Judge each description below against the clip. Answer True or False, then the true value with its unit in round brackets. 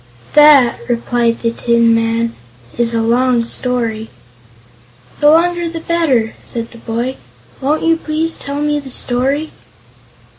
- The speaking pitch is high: True (250 Hz)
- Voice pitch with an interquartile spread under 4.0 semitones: False (4.4 semitones)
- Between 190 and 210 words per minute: False (135 wpm)